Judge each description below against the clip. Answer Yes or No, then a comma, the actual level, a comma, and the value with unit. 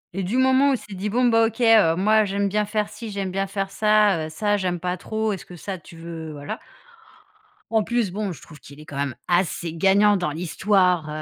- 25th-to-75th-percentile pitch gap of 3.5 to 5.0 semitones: Yes, average, 3.8 semitones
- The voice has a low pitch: No, high, 195 Hz